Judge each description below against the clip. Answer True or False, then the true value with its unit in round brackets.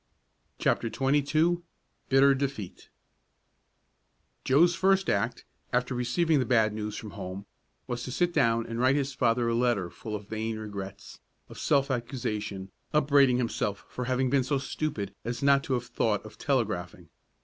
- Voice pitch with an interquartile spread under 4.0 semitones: False (4.3 semitones)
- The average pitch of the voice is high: False (125 Hz)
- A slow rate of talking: False (155 wpm)